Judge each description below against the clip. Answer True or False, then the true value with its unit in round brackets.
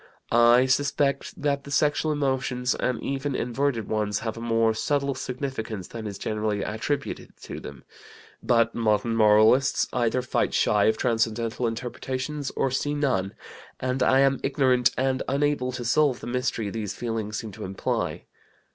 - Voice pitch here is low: True (125 Hz)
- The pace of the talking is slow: False (155 wpm)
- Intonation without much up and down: False (3.4 semitones)